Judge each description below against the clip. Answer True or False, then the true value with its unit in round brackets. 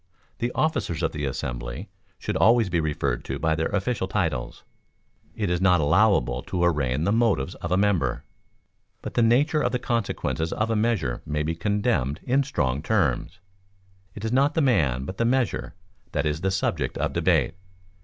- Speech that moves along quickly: False (175 wpm)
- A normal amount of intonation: False (7.4 semitones)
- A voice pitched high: False (95 Hz)